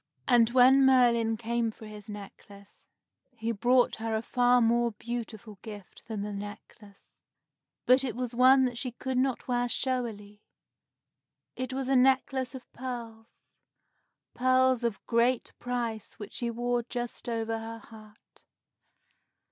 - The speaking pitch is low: No, high, 235 Hz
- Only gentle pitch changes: Yes, narrow, 2.2 semitones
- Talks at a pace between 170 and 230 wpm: No, average, 140 wpm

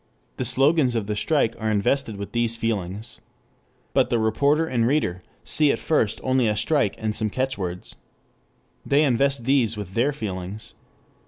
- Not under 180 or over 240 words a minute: No, average, 160 wpm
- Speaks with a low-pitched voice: Yes, low, 115 Hz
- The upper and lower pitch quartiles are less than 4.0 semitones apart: No, average, 4.4 semitones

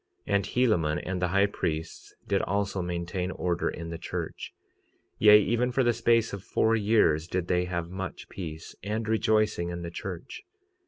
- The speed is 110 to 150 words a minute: No, average, 175 wpm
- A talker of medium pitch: No, very low, 95 Hz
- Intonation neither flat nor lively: Yes, average, 3.8 semitones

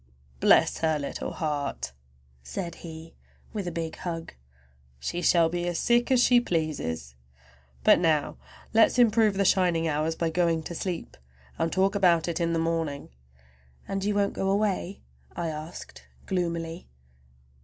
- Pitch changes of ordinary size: Yes, average, 3.1 semitones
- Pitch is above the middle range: No, medium, 170 Hz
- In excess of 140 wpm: Yes, average, 150 wpm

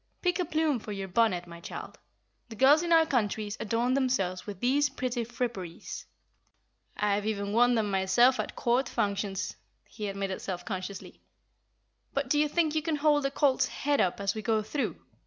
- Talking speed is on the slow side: No, average, 180 wpm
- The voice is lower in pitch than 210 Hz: No, high, 230 Hz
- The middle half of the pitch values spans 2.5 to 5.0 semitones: No, wide, 5.6 semitones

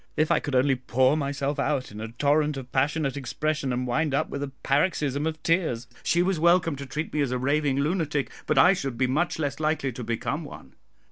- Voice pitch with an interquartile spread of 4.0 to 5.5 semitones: No, average, 2.9 semitones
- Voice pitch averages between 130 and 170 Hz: Yes, medium, 140 Hz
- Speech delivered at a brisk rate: Yes, fast, 220 wpm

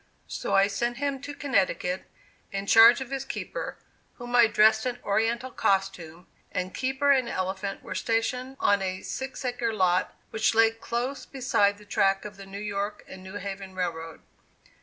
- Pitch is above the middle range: Yes, high, 210 Hz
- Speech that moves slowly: No, average, 170 wpm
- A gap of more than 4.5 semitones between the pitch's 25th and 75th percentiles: No, average, 4.0 semitones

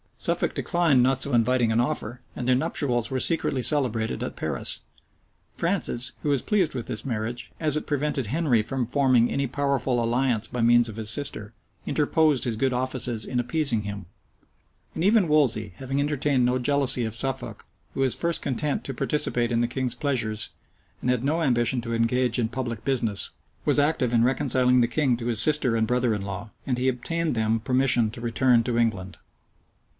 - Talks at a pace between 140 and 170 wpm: No, average, 185 wpm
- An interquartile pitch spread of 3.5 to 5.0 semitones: No, average, 3.1 semitones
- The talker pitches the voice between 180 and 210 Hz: No, low, 125 Hz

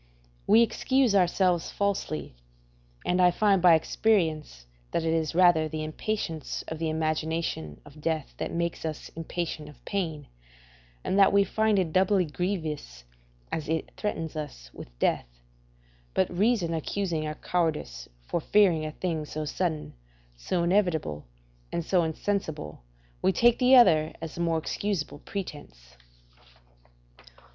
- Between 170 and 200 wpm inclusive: No, average, 140 wpm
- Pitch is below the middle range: No, medium, 165 Hz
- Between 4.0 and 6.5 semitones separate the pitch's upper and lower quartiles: No, average, 3.6 semitones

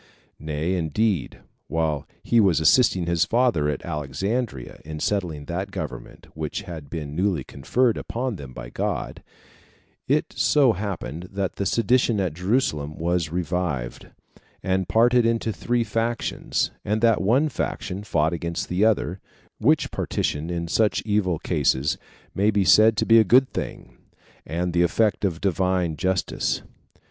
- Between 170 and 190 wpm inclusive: No, average, 145 wpm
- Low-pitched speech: Yes, very low, 90 Hz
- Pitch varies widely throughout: Yes, wide, 5.7 semitones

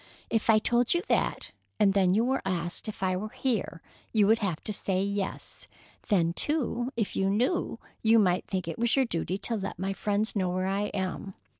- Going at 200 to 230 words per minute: Yes, fast, 205 wpm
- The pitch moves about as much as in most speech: Yes, average, 3.2 semitones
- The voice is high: Yes, high, 200 Hz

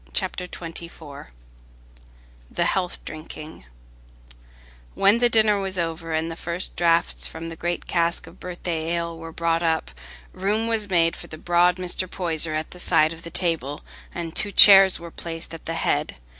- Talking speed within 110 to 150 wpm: No, average, 170 wpm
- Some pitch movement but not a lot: No, narrow, 1.9 semitones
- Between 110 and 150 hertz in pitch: No, medium, 170 Hz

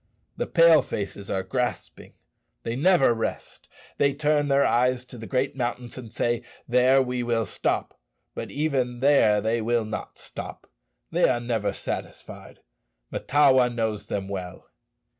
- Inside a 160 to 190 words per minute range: No, average, 145 wpm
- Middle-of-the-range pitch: No, low, 125 Hz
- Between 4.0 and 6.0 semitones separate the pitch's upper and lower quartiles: No, average, 3.1 semitones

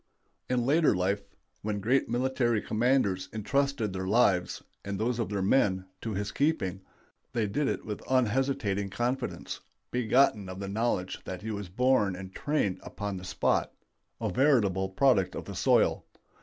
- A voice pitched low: Yes, low, 105 Hz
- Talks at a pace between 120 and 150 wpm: No, average, 160 wpm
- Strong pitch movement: No, average, 4.8 semitones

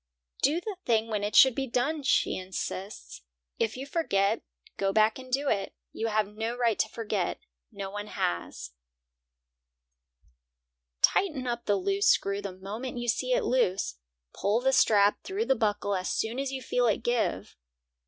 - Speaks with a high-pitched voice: Yes, high, 225 Hz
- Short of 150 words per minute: No, average, 175 wpm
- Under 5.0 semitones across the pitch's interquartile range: Yes, average, 4.5 semitones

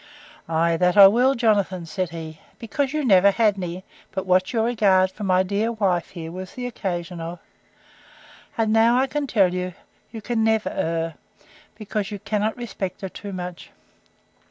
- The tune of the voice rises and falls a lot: No, average, 3.7 semitones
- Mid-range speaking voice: No, high, 195 Hz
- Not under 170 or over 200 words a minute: Yes, average, 175 wpm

